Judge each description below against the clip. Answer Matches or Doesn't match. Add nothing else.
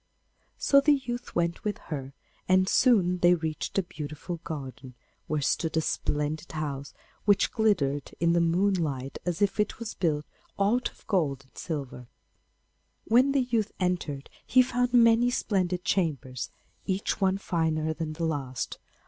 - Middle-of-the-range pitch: Matches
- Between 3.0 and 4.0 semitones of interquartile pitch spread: Doesn't match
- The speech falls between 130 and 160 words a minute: Matches